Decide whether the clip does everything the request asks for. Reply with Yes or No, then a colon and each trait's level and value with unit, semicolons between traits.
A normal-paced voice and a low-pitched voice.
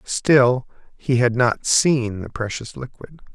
Yes: average, 145 wpm; low, 120 Hz